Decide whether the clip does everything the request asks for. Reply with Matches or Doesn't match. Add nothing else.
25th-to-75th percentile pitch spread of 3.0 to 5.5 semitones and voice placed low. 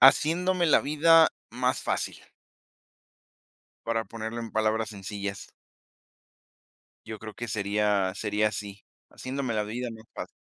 Matches